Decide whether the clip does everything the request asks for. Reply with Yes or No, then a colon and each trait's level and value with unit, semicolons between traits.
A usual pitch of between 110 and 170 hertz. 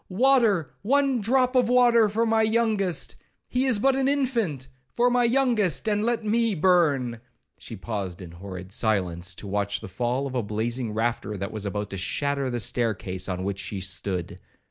Yes: low, 135 Hz